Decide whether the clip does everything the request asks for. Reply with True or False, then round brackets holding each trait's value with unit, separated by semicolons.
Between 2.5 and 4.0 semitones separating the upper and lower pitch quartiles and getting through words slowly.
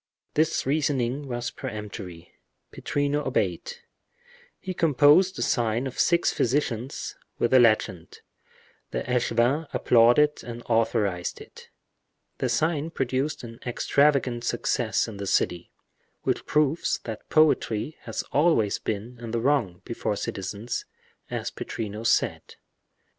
False (4.7 semitones; 115 wpm)